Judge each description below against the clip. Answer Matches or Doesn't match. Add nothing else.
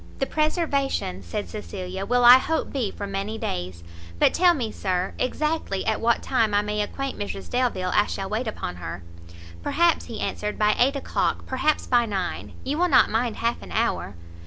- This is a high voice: Matches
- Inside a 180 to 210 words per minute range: Matches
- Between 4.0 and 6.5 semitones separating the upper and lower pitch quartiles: Matches